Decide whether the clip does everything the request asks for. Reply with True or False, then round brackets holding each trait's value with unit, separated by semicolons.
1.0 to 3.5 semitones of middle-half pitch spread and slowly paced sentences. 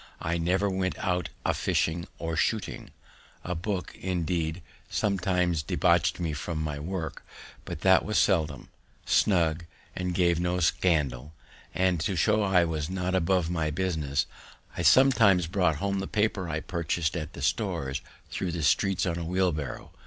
False (2.7 semitones; 160 wpm)